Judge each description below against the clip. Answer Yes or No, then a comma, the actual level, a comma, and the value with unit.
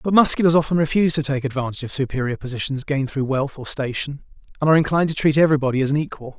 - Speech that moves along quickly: Yes, fast, 225 wpm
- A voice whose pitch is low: No, medium, 145 Hz